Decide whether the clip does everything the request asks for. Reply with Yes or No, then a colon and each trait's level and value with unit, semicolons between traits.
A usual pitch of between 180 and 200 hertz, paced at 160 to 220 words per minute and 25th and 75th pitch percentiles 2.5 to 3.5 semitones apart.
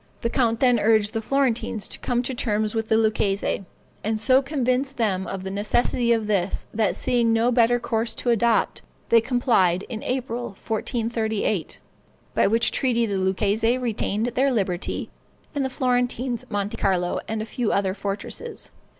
No: high, 225 Hz; average, 165 wpm; average, 3.0 semitones